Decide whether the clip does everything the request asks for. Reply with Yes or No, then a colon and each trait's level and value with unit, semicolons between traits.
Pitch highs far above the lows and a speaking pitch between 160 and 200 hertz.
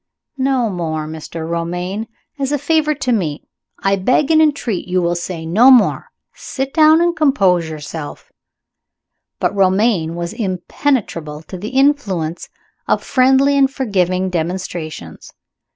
Yes: wide, 7.9 semitones; high, 190 Hz